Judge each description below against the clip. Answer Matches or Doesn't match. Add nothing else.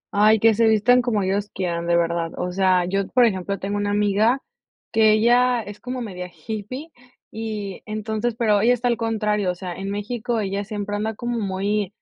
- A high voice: Matches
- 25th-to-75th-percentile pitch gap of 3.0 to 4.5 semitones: Doesn't match